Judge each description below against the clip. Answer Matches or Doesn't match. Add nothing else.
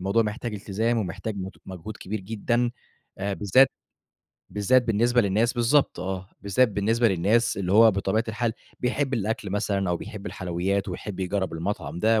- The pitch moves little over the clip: Doesn't match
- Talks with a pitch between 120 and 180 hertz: Doesn't match